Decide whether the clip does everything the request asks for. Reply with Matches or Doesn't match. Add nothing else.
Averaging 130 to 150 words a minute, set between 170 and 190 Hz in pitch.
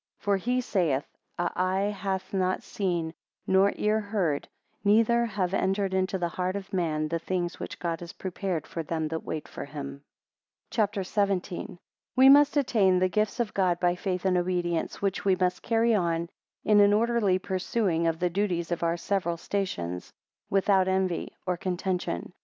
Doesn't match